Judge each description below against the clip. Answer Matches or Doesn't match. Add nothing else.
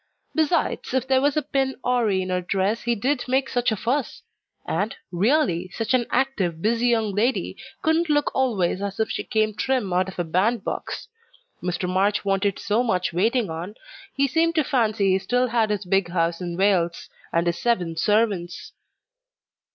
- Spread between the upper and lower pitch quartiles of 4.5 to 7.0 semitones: Matches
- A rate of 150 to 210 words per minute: Matches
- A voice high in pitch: Matches